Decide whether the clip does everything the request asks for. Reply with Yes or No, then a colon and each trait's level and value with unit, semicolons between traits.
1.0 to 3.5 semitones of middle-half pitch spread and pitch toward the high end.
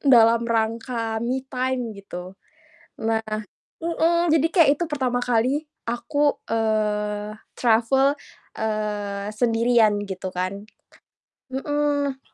No: average, 4.0 semitones; high, 230 Hz